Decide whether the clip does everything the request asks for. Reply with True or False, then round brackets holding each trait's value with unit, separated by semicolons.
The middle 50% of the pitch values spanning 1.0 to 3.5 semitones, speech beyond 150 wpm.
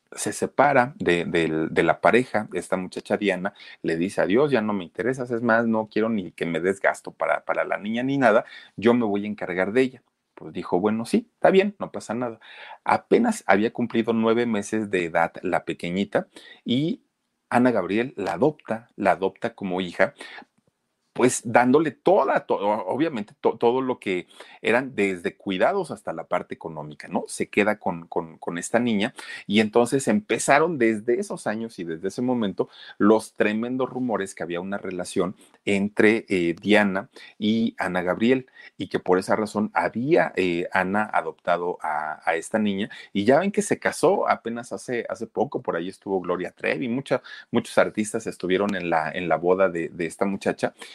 False (4.2 semitones; 180 wpm)